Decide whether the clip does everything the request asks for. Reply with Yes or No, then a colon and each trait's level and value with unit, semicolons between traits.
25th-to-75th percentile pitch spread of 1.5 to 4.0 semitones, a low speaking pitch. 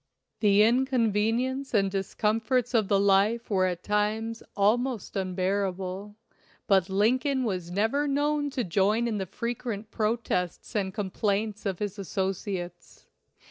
No: average, 3.3 semitones; high, 210 Hz